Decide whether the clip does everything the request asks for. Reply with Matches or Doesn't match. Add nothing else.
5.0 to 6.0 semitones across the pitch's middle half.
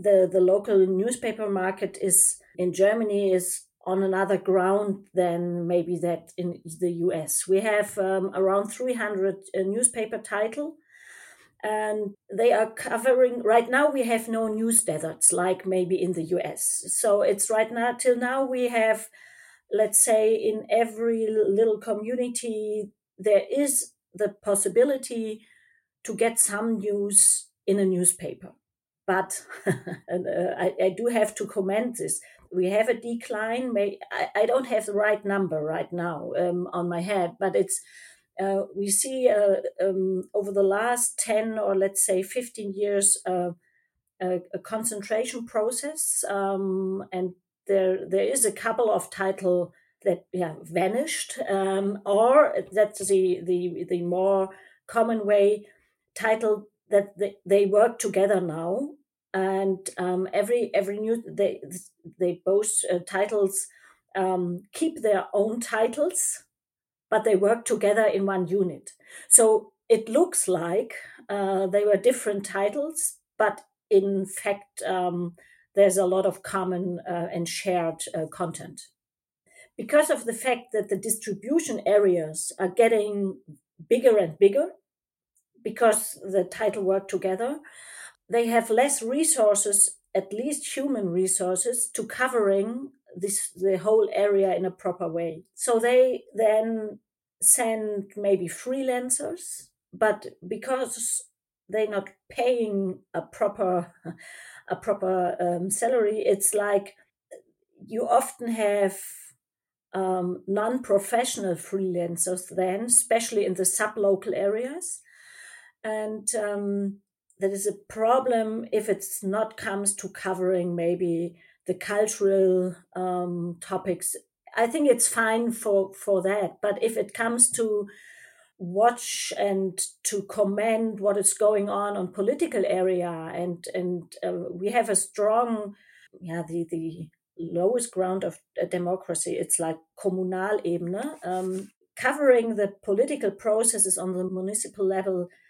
Doesn't match